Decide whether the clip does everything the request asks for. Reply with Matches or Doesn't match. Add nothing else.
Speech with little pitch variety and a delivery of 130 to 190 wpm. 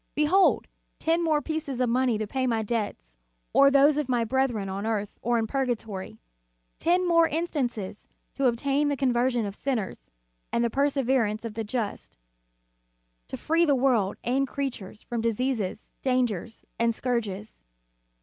Doesn't match